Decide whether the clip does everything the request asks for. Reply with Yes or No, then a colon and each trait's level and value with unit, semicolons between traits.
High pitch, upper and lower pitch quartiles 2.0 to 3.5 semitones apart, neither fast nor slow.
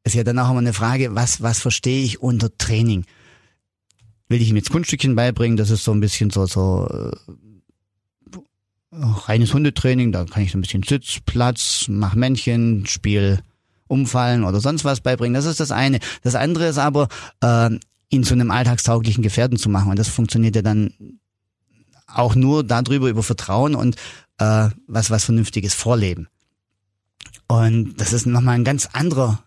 No: low, 115 Hz; average, 3.2 semitones; average, 170 wpm